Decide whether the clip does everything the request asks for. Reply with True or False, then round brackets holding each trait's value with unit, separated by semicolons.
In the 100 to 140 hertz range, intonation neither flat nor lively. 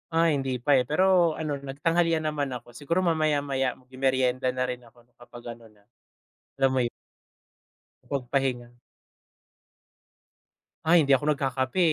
True (135 Hz; 3.4 semitones)